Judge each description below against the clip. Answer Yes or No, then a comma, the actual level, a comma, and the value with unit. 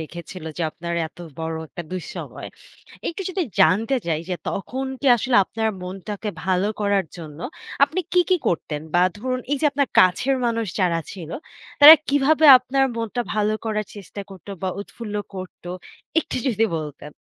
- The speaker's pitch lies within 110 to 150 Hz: No, high, 205 Hz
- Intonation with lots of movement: Yes, wide, 6.4 semitones